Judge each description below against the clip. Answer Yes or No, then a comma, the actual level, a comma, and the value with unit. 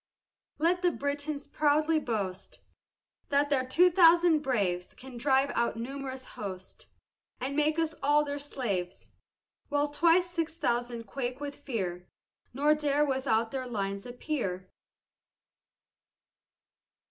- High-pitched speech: Yes, very high, 275 Hz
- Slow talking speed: Yes, slow, 115 wpm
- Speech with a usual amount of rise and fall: Yes, average, 4.2 semitones